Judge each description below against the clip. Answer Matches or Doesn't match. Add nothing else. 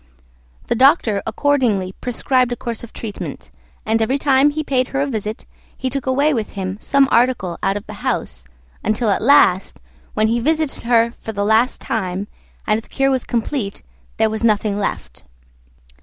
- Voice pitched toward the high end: Matches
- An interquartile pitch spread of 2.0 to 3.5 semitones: Doesn't match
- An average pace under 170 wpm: Doesn't match